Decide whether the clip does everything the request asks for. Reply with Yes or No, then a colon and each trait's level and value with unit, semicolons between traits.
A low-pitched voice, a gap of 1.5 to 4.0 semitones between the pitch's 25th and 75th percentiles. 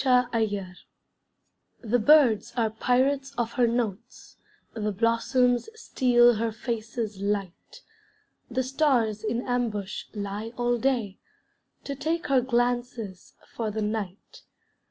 No: high, 235 Hz; average, 2.7 semitones